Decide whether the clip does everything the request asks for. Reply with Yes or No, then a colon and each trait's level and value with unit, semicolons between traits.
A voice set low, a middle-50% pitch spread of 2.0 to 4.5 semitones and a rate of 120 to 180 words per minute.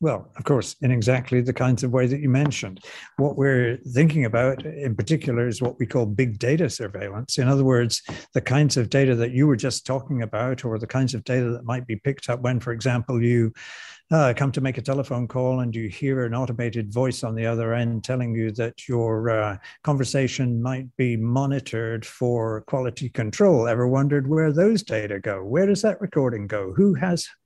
No: low, 125 Hz; narrow, 2.6 semitones; fast, 205 wpm